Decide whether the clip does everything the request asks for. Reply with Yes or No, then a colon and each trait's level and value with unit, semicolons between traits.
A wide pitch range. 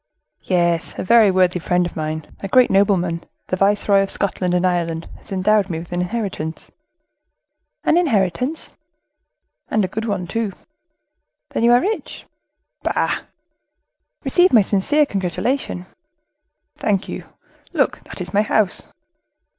No: average, 3.7 semitones